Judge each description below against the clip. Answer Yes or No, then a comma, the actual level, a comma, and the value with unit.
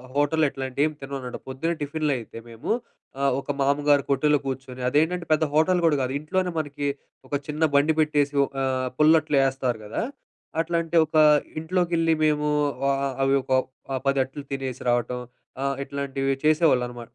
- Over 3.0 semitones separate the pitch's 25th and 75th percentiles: No, average, 2.7 semitones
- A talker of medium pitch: Yes, medium, 145 Hz